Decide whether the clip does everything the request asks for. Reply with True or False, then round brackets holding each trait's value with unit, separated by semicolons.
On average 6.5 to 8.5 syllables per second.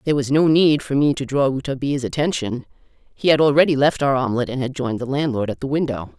True (6.8 syllables/s)